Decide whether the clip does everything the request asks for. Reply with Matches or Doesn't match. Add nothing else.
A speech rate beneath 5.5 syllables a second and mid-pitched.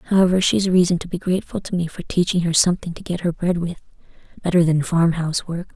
Doesn't match